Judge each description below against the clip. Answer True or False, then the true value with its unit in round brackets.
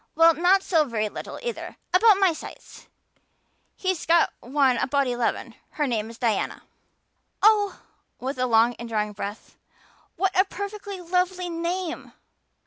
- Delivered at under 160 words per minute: True (140 wpm)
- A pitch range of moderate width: False (7.5 semitones)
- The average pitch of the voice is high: True (330 Hz)